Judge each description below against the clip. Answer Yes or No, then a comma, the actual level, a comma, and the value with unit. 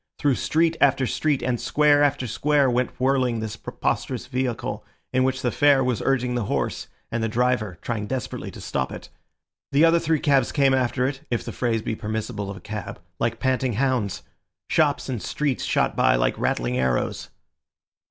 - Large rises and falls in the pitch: No, average, 3.5 semitones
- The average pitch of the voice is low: Yes, low, 125 Hz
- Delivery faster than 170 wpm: Yes, average, 180 wpm